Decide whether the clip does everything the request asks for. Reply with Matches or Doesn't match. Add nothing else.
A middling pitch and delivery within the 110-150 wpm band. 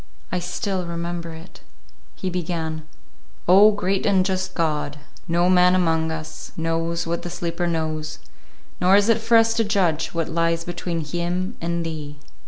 Doesn't match